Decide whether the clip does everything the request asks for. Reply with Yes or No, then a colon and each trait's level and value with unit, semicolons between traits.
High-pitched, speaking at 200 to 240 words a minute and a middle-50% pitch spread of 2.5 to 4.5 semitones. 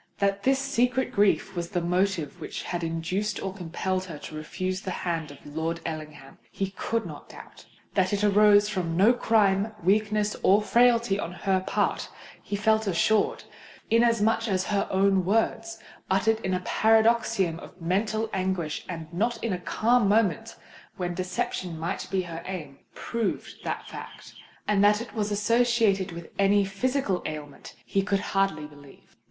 No: high, 195 Hz; average, 155 wpm; average, 3.7 semitones